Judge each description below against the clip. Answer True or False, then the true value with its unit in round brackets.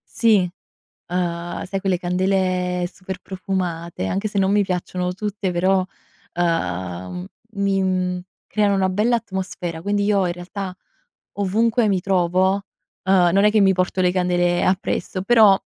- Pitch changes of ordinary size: False (1.9 semitones)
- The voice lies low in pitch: False (185 Hz)